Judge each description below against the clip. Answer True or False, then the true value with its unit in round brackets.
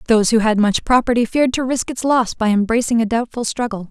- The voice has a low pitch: False (235 Hz)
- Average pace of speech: False (230 wpm)